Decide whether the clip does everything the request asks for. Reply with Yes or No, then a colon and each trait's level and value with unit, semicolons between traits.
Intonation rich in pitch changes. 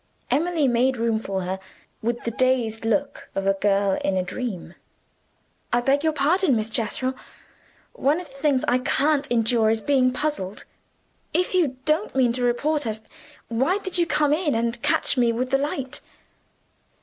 No: average, 4.5 semitones